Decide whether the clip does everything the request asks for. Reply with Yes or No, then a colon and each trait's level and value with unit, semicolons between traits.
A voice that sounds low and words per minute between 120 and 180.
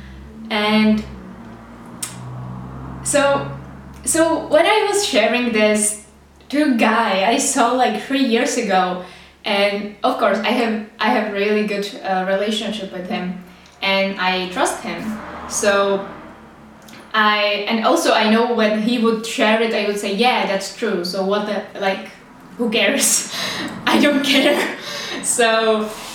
No: high, 215 Hz; average, 140 wpm